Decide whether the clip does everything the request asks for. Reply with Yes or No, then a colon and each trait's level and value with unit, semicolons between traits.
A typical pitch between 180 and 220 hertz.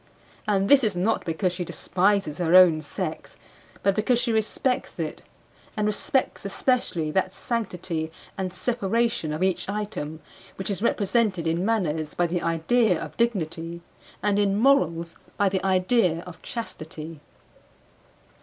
Yes: high, 190 Hz